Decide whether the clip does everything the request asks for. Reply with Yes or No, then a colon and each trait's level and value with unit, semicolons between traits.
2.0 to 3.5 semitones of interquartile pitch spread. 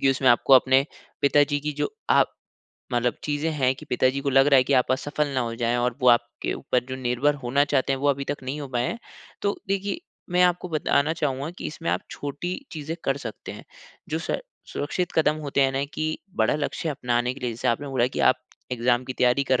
Yes: average, 2.9 semitones